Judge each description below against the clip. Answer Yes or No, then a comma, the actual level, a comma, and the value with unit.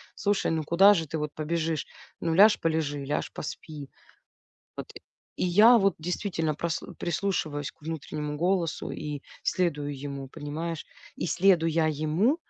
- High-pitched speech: No, medium, 160 Hz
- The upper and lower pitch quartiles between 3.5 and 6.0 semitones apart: No, average, 3.0 semitones